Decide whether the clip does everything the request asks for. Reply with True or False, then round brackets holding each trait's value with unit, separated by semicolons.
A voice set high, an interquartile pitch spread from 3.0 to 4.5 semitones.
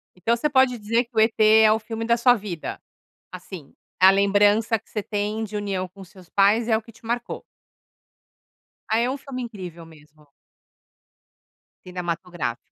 True (210 Hz; 3.8 semitones)